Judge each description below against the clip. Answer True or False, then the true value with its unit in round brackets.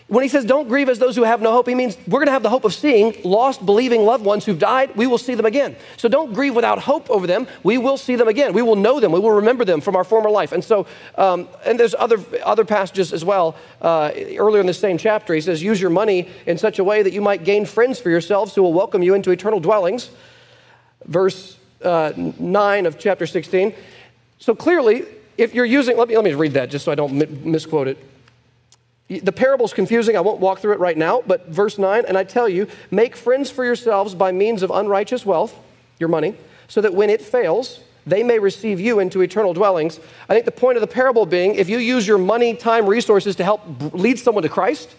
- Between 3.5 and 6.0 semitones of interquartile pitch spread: True (4.6 semitones)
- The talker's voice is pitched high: True (210 Hz)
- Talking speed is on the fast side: True (240 wpm)